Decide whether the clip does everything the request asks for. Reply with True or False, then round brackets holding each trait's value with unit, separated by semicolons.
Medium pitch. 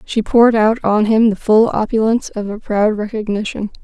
False (215 Hz)